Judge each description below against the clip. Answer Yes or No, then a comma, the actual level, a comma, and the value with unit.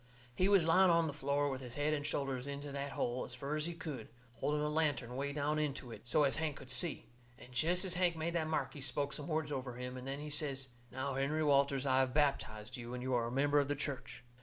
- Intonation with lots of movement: No, average, 2.8 semitones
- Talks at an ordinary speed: No, fast, 260 wpm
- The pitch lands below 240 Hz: Yes, medium, 140 Hz